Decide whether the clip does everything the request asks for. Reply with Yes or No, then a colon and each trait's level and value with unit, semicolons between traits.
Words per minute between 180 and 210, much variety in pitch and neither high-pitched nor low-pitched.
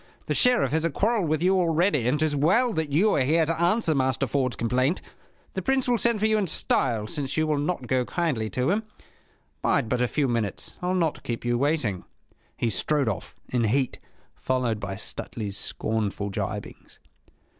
Yes: average, 190 wpm; wide, 6.2 semitones; medium, 145 Hz